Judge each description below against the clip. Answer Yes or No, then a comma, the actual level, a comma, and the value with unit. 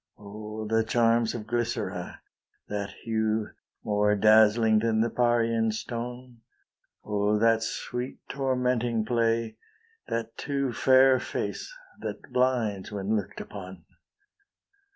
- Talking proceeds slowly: Yes, slow, 110 wpm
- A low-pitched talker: Yes, low, 115 Hz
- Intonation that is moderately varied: No, narrow, 2.0 semitones